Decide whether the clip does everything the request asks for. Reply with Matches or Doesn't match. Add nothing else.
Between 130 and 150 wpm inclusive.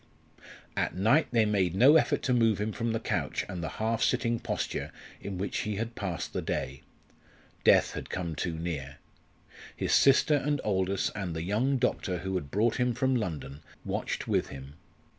Doesn't match